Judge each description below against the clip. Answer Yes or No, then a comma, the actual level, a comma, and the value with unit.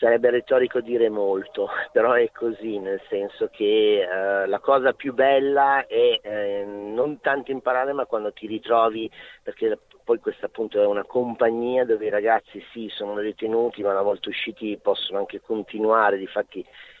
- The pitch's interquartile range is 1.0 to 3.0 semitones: No, average, 4.9 semitones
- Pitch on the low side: Yes, low, 115 Hz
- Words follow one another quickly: No, average, 160 wpm